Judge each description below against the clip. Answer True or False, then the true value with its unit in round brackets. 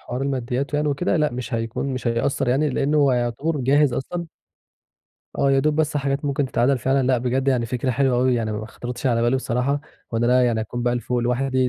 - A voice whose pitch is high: False (130 Hz)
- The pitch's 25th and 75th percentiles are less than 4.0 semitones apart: True (2.4 semitones)